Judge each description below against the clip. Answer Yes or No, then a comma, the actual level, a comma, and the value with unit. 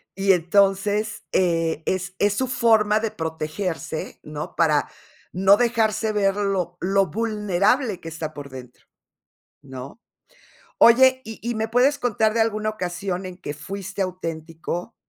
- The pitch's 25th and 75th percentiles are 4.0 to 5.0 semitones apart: Yes, average, 4.5 semitones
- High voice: Yes, high, 195 Hz